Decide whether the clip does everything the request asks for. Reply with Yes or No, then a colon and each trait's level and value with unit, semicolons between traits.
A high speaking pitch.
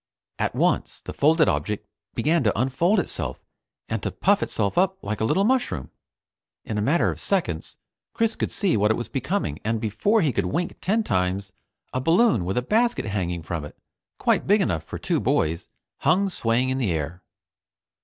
No: low, 125 Hz